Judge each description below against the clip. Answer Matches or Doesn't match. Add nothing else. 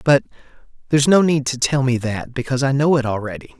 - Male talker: Matches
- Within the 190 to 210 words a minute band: Matches